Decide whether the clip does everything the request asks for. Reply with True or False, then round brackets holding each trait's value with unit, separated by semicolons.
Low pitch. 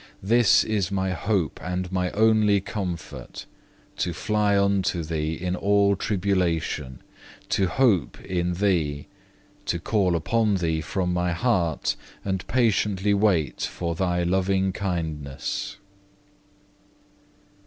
True (95 Hz)